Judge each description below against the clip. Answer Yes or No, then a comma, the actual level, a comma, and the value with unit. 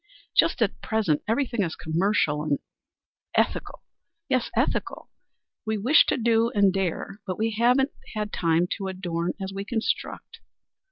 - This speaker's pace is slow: No, average, 145 wpm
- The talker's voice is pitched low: No, high, 200 Hz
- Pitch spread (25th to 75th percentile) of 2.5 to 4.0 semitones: No, average, 4.4 semitones